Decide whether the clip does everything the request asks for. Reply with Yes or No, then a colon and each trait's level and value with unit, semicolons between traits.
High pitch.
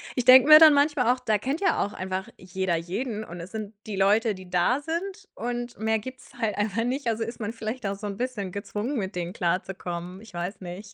Yes: high, 215 Hz